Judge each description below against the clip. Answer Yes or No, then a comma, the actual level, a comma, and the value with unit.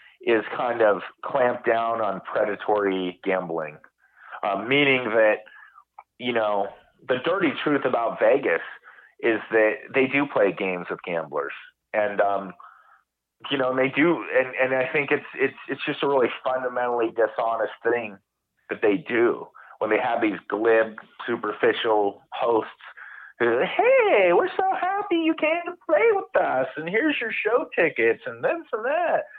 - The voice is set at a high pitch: No, low, 130 Hz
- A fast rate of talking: No, average, 155 wpm